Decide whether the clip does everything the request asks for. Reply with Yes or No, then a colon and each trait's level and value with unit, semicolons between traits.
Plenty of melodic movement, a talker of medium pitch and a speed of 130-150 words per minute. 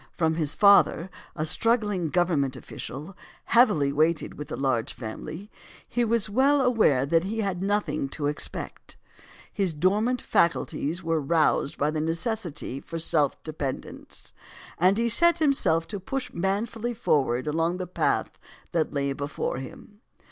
Yes: wide, 6.0 semitones; medium, 170 Hz; average, 145 wpm